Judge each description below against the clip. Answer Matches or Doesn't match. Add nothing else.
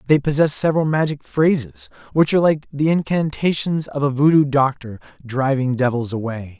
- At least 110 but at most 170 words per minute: Matches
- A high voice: Doesn't match